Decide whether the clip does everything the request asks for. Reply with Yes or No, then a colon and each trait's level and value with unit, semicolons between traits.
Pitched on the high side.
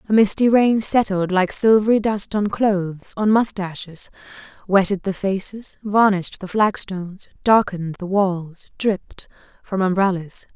Yes: high, 195 Hz